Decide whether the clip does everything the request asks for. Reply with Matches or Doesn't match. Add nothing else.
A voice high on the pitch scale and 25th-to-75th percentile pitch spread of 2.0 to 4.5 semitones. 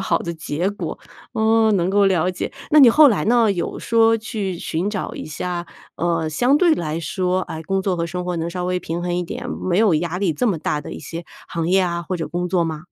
Doesn't match